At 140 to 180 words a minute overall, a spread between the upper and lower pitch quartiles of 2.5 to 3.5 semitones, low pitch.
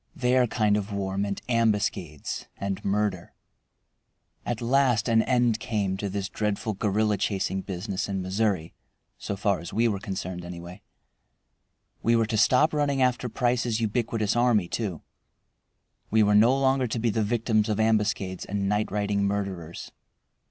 Yes: average, 150 wpm; average, 2.9 semitones; low, 105 Hz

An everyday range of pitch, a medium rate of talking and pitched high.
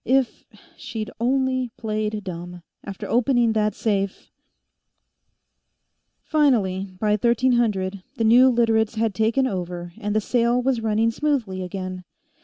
No: average, 3.7 semitones; slow, 120 wpm; high, 220 Hz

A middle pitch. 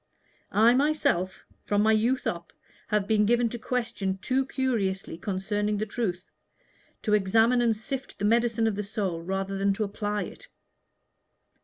No: high, 210 Hz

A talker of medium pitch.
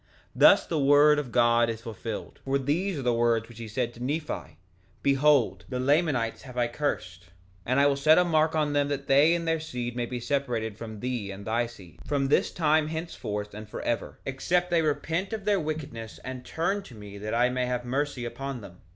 No: low, 130 Hz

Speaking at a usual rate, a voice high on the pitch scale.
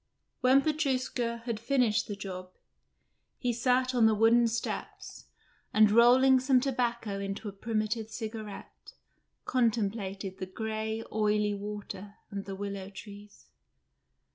No: slow, 120 wpm; high, 220 Hz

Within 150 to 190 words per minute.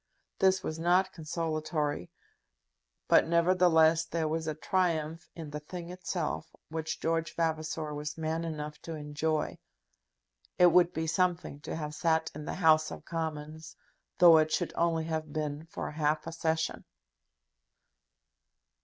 No: average, 140 wpm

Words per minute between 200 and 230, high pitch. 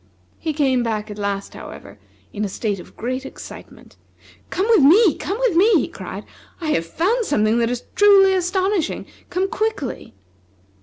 No: average, 165 wpm; very high, 310 Hz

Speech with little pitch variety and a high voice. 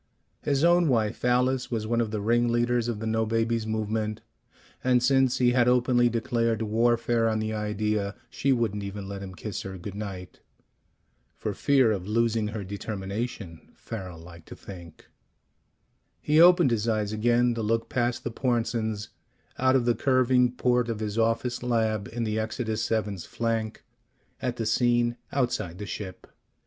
No: narrow, 2.3 semitones; low, 115 Hz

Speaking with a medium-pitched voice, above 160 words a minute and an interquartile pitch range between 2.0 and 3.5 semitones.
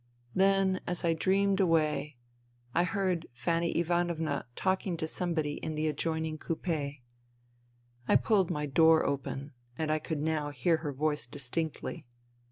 No: medium, 160 Hz; average, 145 wpm; average, 2.7 semitones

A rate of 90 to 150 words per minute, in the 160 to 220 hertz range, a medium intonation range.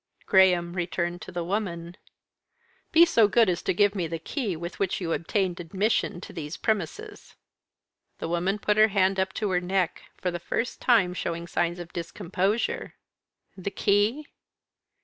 No: average, 165 wpm; medium, 185 Hz; average, 3.2 semitones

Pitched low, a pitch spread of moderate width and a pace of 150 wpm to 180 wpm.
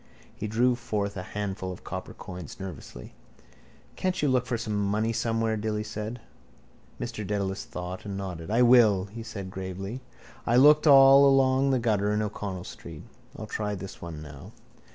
Yes: low, 105 Hz; average, 3.8 semitones; average, 170 wpm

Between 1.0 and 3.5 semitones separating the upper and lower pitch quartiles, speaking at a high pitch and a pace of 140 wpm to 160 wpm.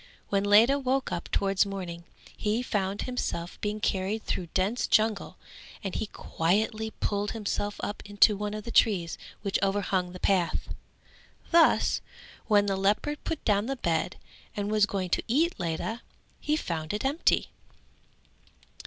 Yes: narrow, 2.6 semitones; high, 205 Hz; average, 150 wpm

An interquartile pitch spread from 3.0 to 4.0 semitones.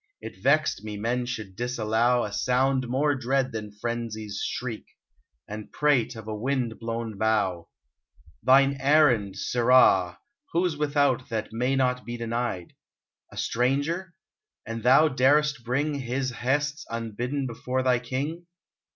Yes: average, 3.4 semitones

